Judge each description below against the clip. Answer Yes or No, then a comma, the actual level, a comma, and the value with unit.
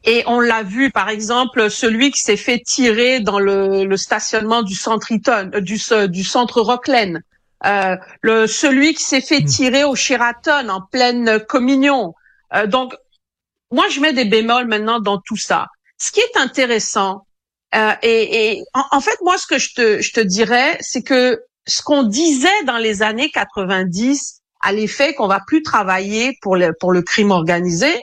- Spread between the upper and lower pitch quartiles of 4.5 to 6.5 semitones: Yes, average, 4.9 semitones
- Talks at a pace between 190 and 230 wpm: No, average, 180 wpm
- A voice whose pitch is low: No, high, 235 Hz